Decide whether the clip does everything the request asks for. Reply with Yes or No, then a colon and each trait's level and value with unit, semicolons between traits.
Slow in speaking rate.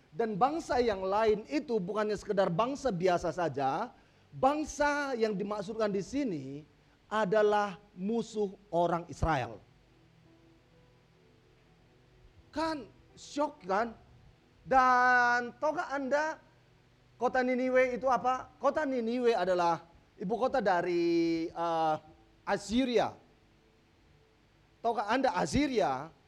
Yes: slow, 90 wpm